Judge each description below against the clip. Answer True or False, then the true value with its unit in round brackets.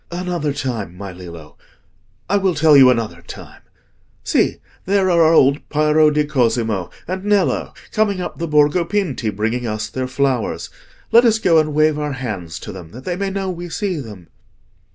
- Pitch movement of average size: False (8.0 semitones)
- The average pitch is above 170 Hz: False (145 Hz)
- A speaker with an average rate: True (175 wpm)